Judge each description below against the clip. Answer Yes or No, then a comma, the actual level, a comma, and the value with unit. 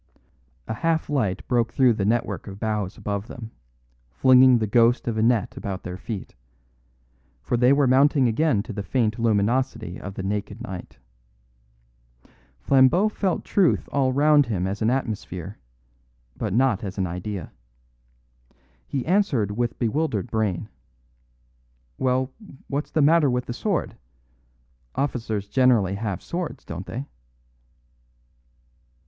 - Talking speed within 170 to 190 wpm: No, slow, 135 wpm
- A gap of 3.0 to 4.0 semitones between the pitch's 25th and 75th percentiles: No, average, 4.6 semitones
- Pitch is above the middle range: No, low, 115 Hz